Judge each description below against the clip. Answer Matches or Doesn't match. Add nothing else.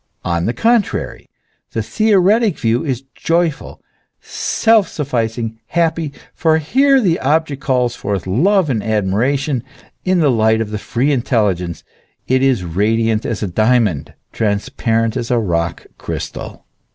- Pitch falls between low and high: Doesn't match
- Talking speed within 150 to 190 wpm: Doesn't match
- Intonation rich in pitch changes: Matches